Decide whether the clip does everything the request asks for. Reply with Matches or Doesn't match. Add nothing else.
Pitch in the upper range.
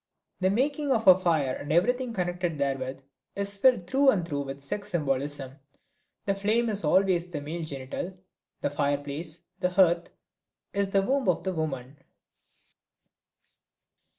Doesn't match